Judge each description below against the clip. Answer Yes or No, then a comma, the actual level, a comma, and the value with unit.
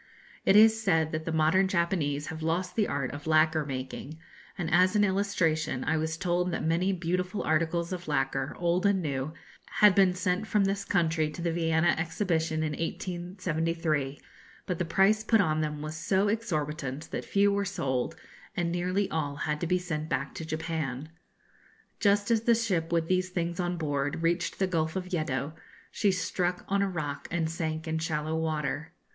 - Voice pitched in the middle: Yes, medium, 165 Hz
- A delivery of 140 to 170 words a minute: No, average, 185 wpm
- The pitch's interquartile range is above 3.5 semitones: No, average, 3.0 semitones